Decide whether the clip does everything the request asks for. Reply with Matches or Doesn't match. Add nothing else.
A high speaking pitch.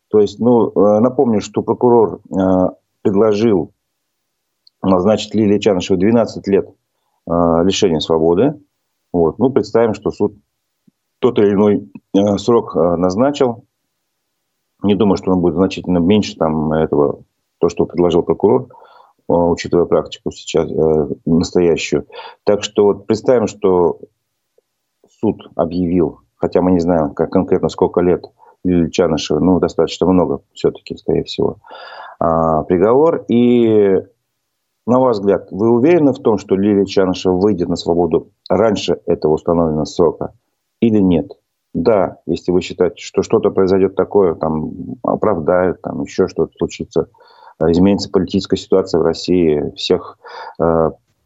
Doesn't match